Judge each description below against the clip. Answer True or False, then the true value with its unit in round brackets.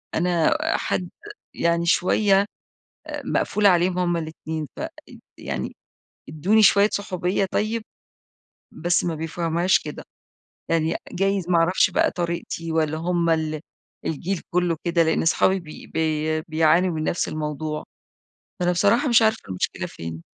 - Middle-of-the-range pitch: True (170 Hz)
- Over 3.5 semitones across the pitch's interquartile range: False (2.7 semitones)